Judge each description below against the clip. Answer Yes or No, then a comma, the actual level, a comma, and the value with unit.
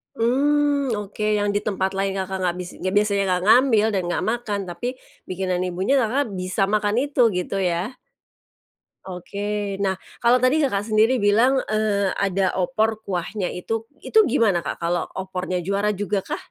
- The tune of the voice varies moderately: Yes, average, 3.3 semitones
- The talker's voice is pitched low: No, high, 205 Hz